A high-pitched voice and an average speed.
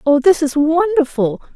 Yes: very high, 310 Hz; average, 155 wpm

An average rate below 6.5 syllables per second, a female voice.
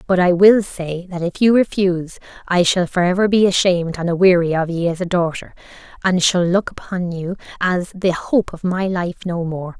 Yes: 5.1 syllables/s; female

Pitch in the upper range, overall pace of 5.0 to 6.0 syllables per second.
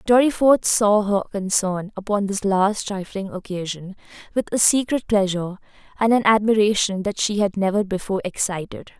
Yes: high, 205 Hz; 5.1 syllables/s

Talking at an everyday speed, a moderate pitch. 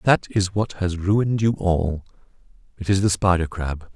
No: average, 165 wpm; very low, 95 Hz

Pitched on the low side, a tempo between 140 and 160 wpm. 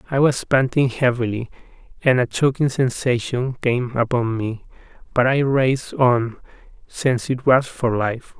Yes: low, 125 Hz; average, 145 wpm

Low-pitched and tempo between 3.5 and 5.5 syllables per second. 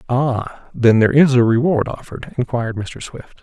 Yes: low, 120 Hz; 5.1 syllables/s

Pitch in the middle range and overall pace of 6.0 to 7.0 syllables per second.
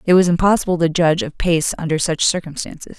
Yes: medium, 170 Hz; 6.3 syllables/s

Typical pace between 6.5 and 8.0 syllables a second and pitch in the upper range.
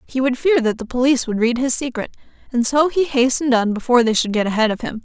Yes: 6.7 syllables/s; very high, 250 Hz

